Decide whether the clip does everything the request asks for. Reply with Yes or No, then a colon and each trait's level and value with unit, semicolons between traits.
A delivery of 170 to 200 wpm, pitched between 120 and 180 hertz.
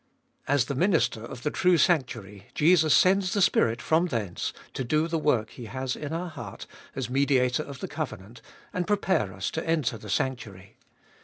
Yes: average, 180 wpm; low, 135 Hz